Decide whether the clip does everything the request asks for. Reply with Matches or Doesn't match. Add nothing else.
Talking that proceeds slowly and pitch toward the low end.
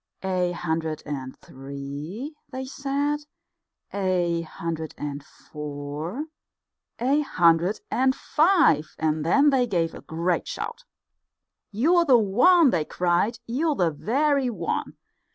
Doesn't match